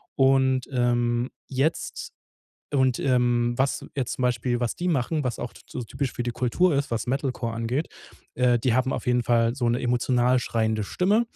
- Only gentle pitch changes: Yes, narrow, 1.8 semitones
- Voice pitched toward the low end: Yes, low, 125 Hz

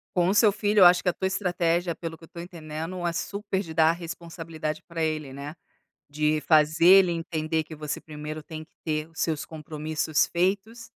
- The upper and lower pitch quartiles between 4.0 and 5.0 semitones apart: No, narrow, 2.4 semitones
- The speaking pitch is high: No, medium, 165 Hz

